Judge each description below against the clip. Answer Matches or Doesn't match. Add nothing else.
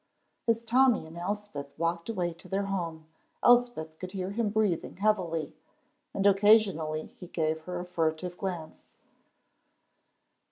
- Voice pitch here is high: Doesn't match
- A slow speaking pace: Matches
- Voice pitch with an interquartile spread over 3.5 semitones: Matches